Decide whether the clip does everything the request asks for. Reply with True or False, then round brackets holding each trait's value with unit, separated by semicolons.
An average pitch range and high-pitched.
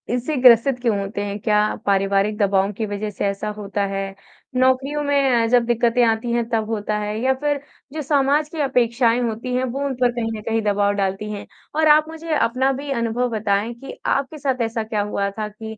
True (3.8 semitones; 230 Hz)